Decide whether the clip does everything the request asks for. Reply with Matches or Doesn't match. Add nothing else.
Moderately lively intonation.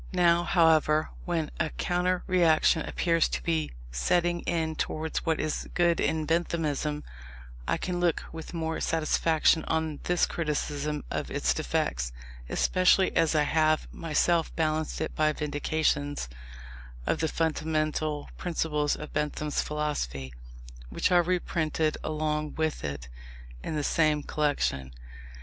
Doesn't match